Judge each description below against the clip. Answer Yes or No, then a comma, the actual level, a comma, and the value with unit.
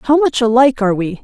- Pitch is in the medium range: No, high, 245 Hz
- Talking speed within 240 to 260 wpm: Yes, fast, 245 wpm